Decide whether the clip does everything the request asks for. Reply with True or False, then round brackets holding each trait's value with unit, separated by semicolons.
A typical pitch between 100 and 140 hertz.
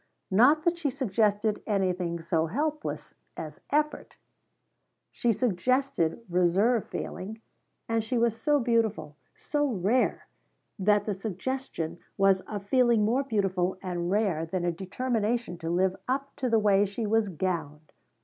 False (210 Hz)